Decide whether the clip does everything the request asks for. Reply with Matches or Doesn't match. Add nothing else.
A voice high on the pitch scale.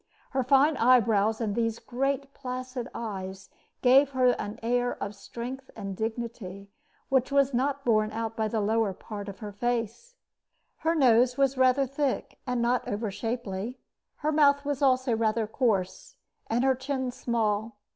Matches